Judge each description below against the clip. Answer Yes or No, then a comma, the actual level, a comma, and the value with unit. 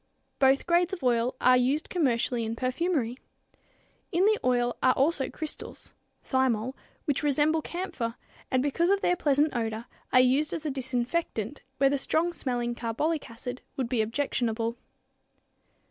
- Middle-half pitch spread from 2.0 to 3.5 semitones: No, average, 4.3 semitones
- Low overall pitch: No, very high, 265 Hz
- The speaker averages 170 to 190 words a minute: No, average, 145 wpm